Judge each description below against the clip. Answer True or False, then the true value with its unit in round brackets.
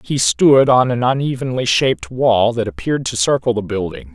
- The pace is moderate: True (190 wpm)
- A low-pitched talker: True (120 Hz)